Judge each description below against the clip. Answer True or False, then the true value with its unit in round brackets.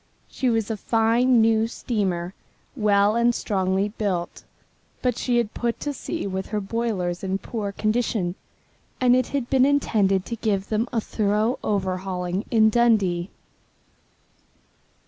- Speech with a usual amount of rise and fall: True (3.5 semitones)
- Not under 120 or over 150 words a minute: True (140 wpm)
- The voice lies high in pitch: True (215 Hz)